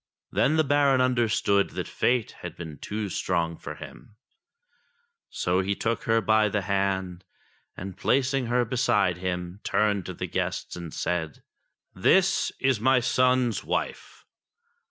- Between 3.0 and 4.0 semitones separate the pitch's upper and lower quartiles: No, wide, 5.6 semitones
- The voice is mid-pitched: No, low, 105 Hz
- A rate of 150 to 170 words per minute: No, average, 140 wpm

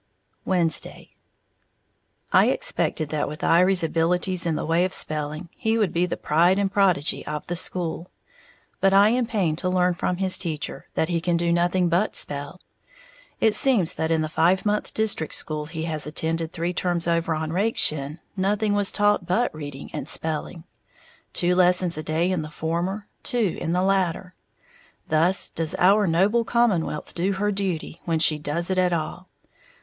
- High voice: No, medium, 175 Hz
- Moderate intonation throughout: Yes, average, 3.1 semitones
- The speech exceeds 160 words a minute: Yes, average, 175 wpm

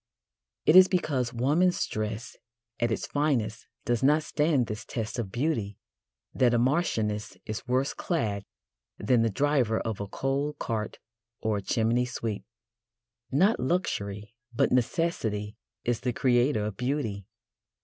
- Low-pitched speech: Yes, low, 120 Hz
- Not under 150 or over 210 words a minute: No, average, 140 wpm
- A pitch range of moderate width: Yes, average, 5.0 semitones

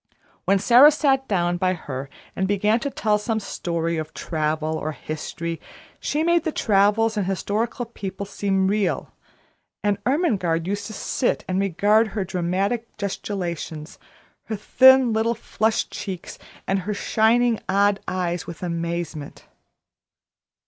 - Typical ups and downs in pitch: Yes, average, 4.3 semitones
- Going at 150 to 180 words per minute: No, slow, 135 wpm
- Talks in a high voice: Yes, high, 200 Hz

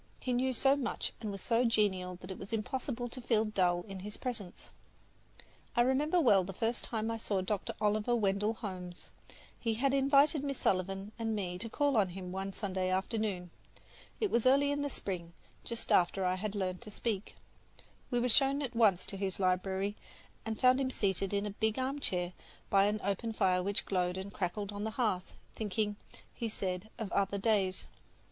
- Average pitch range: Yes, average, 4.0 semitones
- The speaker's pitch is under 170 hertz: No, high, 210 Hz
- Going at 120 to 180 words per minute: No, average, 195 wpm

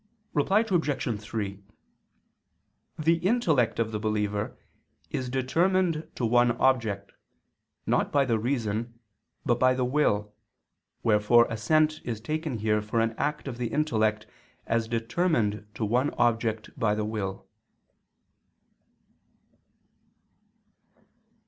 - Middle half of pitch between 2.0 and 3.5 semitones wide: No, average, 5.1 semitones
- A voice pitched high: No, low, 120 Hz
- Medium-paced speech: No, slow, 110 wpm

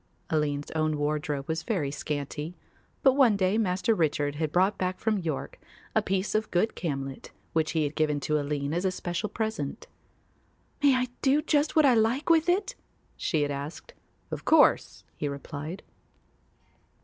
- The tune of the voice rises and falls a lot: Yes, wide, 6.8 semitones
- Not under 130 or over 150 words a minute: No, average, 165 wpm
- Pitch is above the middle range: No, medium, 165 Hz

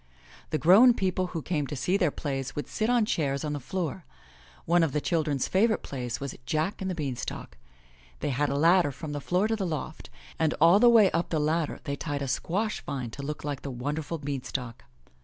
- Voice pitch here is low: No, medium, 155 Hz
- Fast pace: Yes, fast, 215 wpm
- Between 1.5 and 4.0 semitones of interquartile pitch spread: No, average, 4.5 semitones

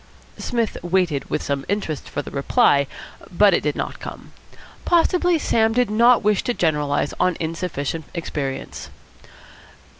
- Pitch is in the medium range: Yes, medium, 180 Hz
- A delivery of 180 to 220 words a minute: No, average, 140 wpm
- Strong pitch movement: Yes, wide, 7.5 semitones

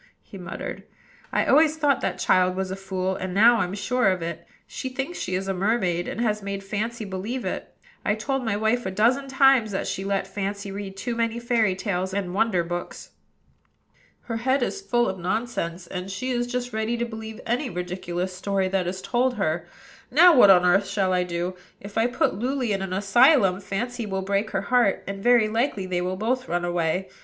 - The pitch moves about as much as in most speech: Yes, average, 4.3 semitones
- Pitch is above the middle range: Yes, high, 200 Hz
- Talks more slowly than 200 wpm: No, fast, 205 wpm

